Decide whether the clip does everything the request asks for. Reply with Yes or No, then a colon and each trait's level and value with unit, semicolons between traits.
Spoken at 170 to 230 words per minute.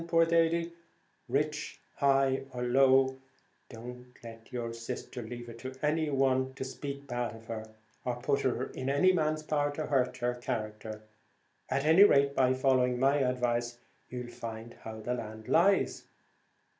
No: average, 155 wpm